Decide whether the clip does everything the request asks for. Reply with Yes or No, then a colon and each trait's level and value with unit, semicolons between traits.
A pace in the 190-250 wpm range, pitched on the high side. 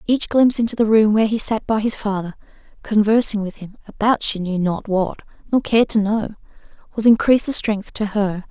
Yes: average, 200 wpm; high, 210 Hz